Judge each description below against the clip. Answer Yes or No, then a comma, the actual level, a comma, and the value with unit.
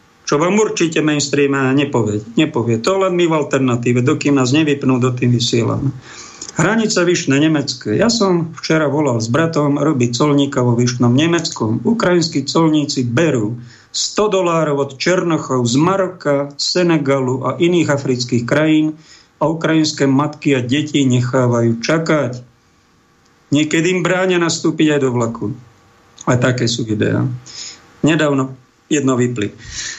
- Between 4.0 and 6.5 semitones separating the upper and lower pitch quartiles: Yes, average, 4.4 semitones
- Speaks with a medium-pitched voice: Yes, medium, 145 Hz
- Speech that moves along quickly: No, average, 130 wpm